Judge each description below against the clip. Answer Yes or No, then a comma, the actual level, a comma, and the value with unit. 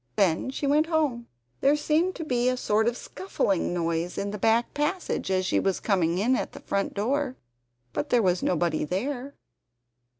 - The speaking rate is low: No, average, 185 wpm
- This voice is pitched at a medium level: No, high, 235 Hz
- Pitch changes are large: Yes, wide, 7.2 semitones